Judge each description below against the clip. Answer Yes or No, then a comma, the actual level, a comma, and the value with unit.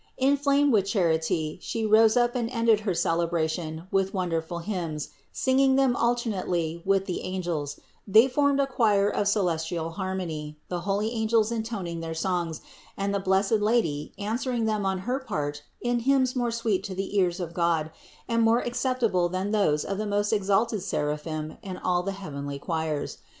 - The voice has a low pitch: No, high, 195 Hz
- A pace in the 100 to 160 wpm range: No, average, 170 wpm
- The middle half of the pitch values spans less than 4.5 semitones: No, average, 5.3 semitones